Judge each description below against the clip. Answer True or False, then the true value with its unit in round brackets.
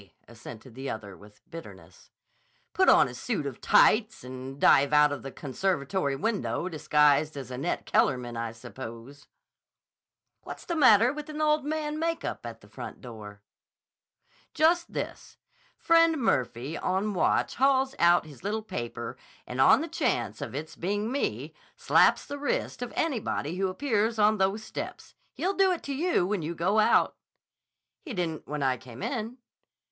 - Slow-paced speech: False (160 wpm)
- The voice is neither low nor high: True (180 Hz)